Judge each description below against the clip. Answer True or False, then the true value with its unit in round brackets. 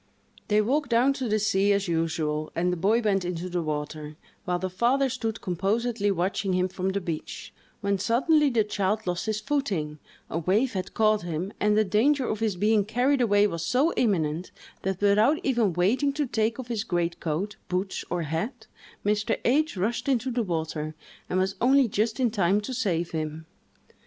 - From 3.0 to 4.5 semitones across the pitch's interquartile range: False (4.9 semitones)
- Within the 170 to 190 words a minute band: True (185 wpm)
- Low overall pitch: False (205 Hz)